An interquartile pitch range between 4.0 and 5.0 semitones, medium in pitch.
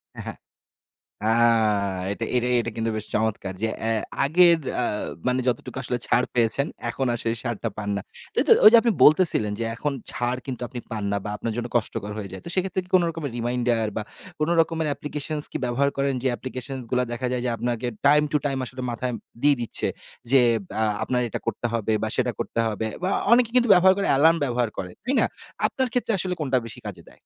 No: average, 4.7 semitones; low, 125 Hz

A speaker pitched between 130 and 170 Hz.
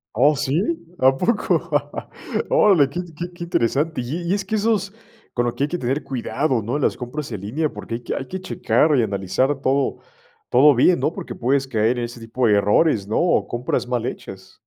Yes: low, 135 Hz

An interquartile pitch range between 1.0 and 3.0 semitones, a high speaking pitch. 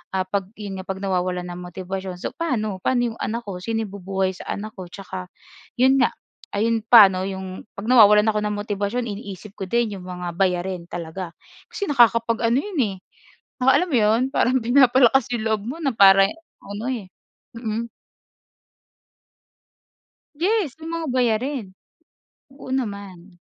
No: average, 4.2 semitones; high, 210 Hz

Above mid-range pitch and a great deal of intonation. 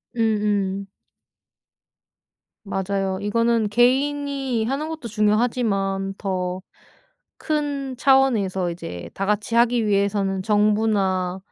No: high, 210 Hz; average, 3.9 semitones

